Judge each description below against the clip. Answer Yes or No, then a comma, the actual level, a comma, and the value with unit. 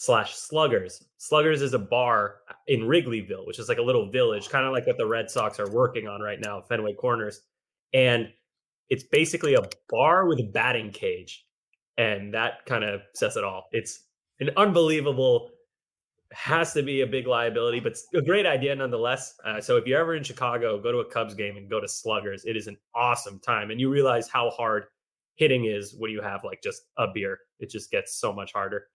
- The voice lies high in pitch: No, medium, 140 Hz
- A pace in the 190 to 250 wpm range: Yes, fast, 205 wpm